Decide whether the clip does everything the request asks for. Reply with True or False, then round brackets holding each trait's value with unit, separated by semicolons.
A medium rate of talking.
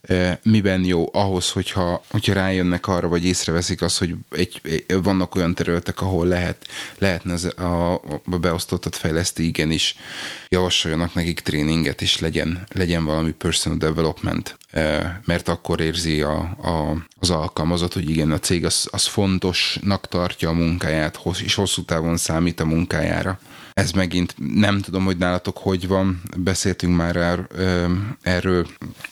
True (140 wpm)